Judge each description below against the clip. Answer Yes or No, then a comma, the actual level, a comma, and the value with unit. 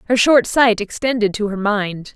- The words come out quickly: No, average, 195 wpm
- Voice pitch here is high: Yes, high, 220 Hz